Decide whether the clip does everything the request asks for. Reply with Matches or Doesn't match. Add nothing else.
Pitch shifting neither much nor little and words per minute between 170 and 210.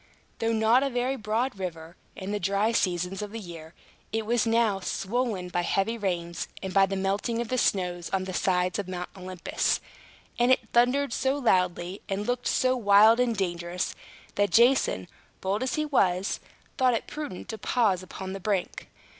Matches